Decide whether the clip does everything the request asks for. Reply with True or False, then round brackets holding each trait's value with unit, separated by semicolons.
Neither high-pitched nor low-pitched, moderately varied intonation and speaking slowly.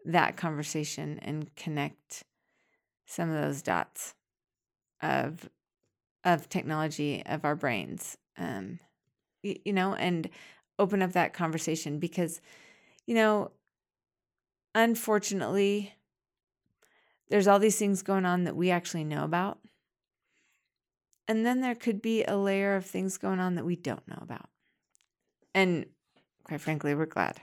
True (180 Hz; 4.4 semitones; 125 wpm)